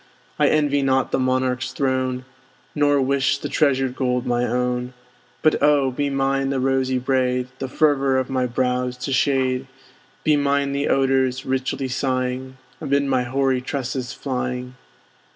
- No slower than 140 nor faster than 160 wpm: Yes, average, 150 wpm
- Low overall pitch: Yes, low, 130 Hz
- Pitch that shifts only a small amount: Yes, narrow, 1.4 semitones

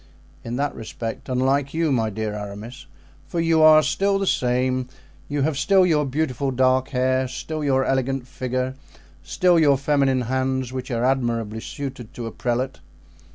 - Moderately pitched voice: No, low, 130 Hz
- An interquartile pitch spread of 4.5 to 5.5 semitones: No, narrow, 2.5 semitones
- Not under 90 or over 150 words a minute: No, average, 160 wpm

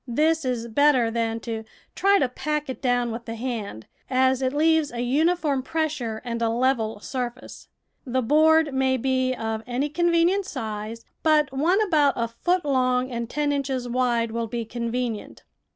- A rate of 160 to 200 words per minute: Yes, average, 170 wpm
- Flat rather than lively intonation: No, average, 4.2 semitones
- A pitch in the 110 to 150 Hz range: No, very high, 255 Hz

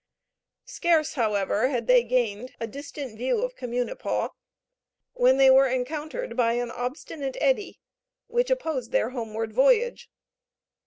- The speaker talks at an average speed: No, slow, 125 wpm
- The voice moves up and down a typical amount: Yes, average, 4.2 semitones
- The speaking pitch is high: Yes, very high, 255 Hz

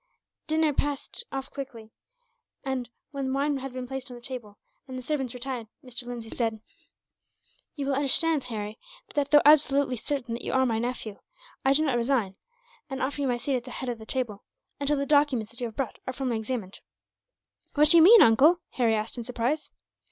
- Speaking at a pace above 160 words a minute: Yes, average, 200 wpm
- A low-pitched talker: No, very high, 260 Hz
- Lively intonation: No, average, 3.0 semitones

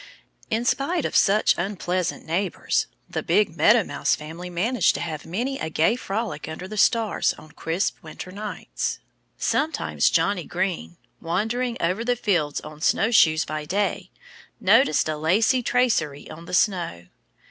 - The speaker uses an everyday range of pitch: No, wide, 5.9 semitones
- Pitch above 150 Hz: Yes, medium, 185 Hz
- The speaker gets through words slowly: No, average, 150 wpm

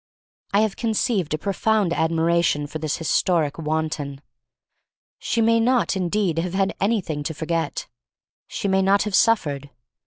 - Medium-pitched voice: Yes, medium, 170 Hz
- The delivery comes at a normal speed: Yes, average, 155 wpm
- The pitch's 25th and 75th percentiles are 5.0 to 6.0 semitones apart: No, average, 4.6 semitones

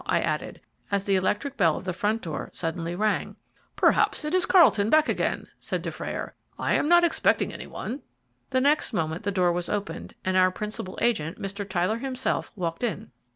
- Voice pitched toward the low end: No, high, 200 Hz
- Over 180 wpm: Yes, average, 190 wpm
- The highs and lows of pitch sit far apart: Yes, wide, 5.9 semitones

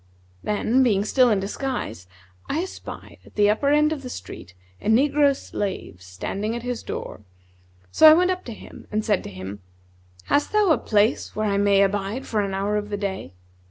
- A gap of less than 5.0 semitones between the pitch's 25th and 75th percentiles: No, average, 5.3 semitones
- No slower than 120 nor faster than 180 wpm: No, average, 195 wpm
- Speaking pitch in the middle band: No, high, 215 Hz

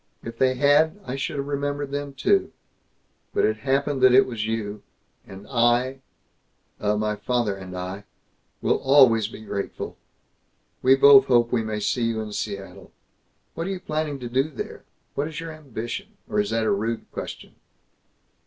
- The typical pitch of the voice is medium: No, low, 125 Hz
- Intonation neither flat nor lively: Yes, average, 4.6 semitones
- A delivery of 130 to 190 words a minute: Yes, average, 170 wpm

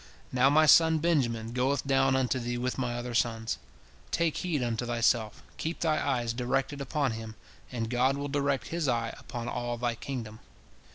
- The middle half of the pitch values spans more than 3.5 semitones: No, average, 3.0 semitones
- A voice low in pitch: Yes, low, 125 Hz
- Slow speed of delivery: No, average, 175 wpm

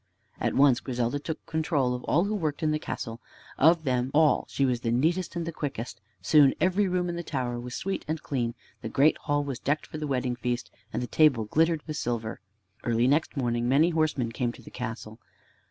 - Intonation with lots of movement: No, average, 4.4 semitones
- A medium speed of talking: No, fast, 215 wpm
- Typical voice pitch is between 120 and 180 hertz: Yes, medium, 140 Hz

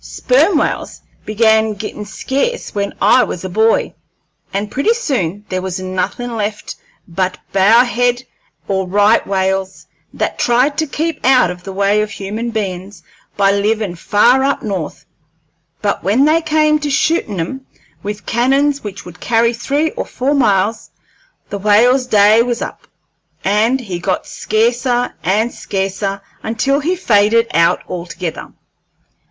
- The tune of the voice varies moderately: Yes, average, 4.4 semitones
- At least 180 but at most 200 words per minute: No, average, 145 wpm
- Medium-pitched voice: No, high, 215 Hz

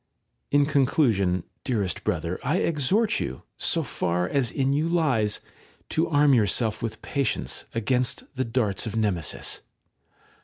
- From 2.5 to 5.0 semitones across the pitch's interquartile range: No, wide, 5.6 semitones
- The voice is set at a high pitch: No, low, 125 Hz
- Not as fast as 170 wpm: Yes, average, 150 wpm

